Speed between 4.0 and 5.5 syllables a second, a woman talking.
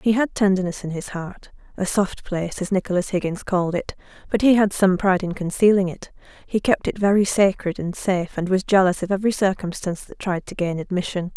No: 5.9 syllables/s; female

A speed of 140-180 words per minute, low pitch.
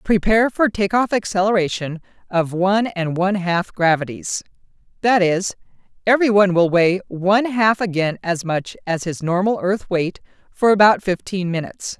No: average, 145 wpm; high, 190 Hz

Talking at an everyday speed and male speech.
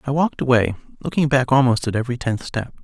No: fast, 210 wpm; male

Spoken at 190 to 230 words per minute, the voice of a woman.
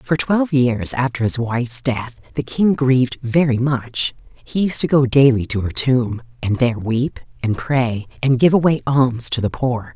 Yes: average, 195 wpm; female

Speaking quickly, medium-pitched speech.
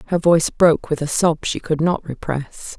Yes: fast, 215 wpm; medium, 160 Hz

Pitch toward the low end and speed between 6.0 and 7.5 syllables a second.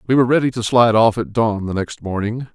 Yes: low, 115 Hz; 6.4 syllables/s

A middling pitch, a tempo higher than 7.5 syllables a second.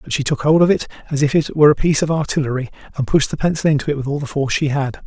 Yes: medium, 145 Hz; 7.7 syllables/s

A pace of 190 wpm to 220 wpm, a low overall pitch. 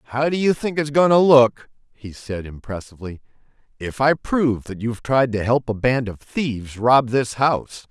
Yes: fast, 205 wpm; low, 125 Hz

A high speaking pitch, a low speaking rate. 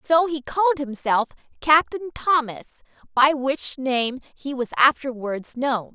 Yes: very high, 275 Hz; slow, 130 wpm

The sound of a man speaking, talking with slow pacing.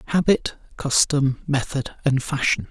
Yes: male; slow, 110 wpm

